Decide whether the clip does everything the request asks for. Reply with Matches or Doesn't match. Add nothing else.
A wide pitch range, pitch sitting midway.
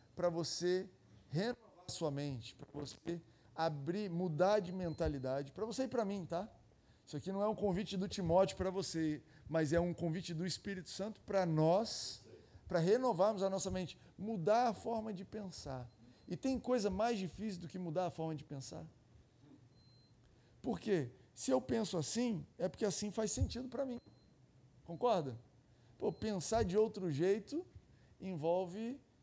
Matches